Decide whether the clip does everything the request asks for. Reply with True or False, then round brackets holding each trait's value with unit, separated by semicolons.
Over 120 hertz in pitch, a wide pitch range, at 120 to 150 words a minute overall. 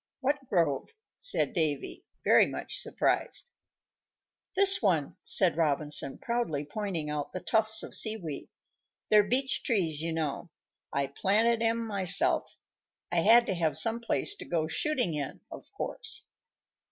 True (190 Hz; 6.9 semitones; 140 wpm)